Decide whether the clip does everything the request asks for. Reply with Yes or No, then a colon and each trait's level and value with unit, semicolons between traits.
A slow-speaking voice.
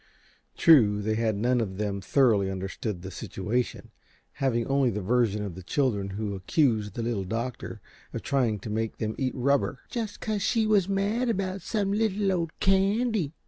No: average, 175 wpm